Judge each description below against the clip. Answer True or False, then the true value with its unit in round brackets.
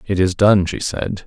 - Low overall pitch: True (95 Hz)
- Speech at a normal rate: False (235 wpm)